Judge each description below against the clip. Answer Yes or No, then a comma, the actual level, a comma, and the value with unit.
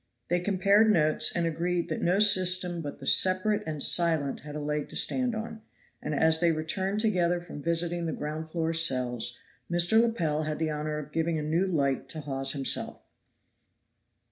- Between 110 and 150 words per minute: No, average, 180 wpm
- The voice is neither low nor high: Yes, medium, 165 Hz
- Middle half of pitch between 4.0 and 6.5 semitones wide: No, average, 3.2 semitones